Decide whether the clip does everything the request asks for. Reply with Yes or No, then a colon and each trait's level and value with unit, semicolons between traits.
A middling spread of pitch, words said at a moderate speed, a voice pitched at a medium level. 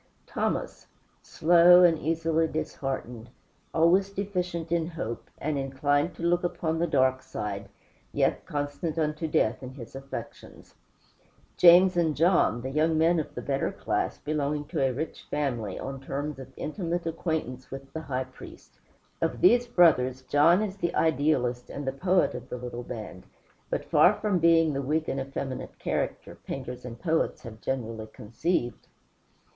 Yes: average, 4.3 semitones; average, 155 wpm; medium, 150 Hz